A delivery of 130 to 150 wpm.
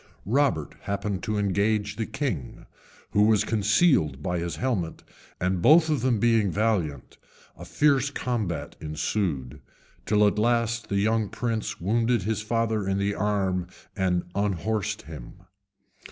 Yes: average, 140 wpm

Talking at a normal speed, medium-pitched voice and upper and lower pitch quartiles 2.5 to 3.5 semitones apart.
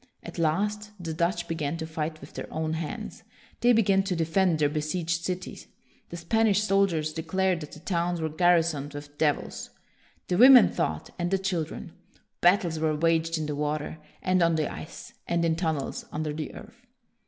Yes: average, 185 wpm; medium, 165 Hz; average, 2.8 semitones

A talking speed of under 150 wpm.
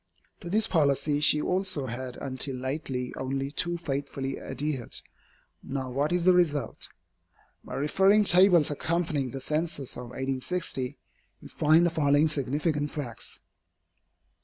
Yes: slow, 135 wpm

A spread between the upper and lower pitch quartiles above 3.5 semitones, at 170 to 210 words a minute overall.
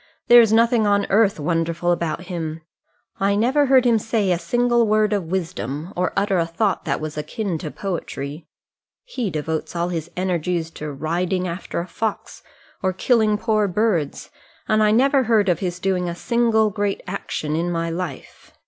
Yes: average, 4.5 semitones; average, 175 wpm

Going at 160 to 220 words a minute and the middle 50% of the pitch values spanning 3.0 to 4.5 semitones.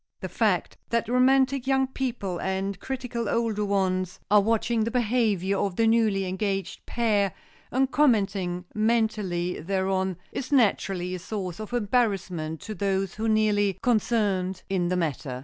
No: average, 145 wpm; average, 3.6 semitones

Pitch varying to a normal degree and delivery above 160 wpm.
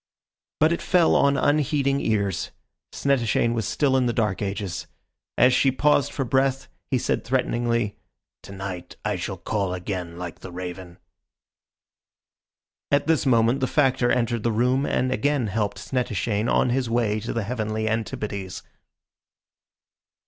No: average, 4.6 semitones; average, 145 wpm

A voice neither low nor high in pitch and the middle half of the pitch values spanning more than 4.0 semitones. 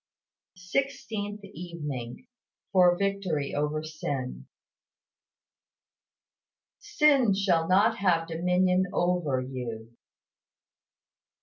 Yes: medium, 180 Hz; average, 5.0 semitones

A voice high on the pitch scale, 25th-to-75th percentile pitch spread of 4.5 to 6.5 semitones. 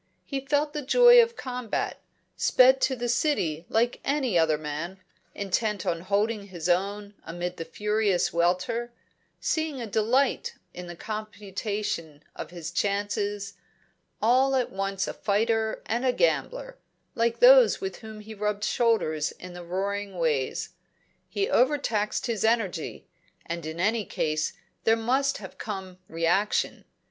Yes: high, 210 Hz; average, 5.1 semitones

